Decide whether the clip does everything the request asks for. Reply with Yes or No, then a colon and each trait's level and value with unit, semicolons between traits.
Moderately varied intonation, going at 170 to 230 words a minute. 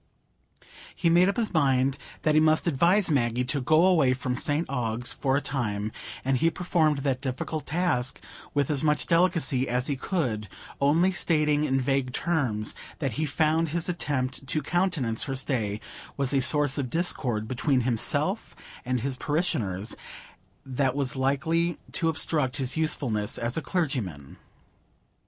No: average, 4.0 semitones; average, 155 wpm